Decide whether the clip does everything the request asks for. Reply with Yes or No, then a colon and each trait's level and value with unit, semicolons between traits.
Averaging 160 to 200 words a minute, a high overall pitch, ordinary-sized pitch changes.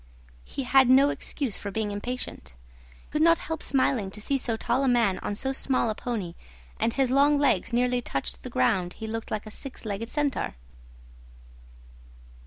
Yes: average, 190 wpm; high, 240 Hz; average, 4.6 semitones